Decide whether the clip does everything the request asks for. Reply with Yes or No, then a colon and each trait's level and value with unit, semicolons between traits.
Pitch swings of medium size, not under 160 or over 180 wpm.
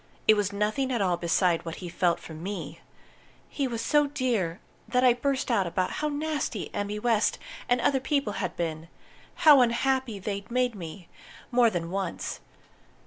No: wide, 6.0 semitones; average, 170 wpm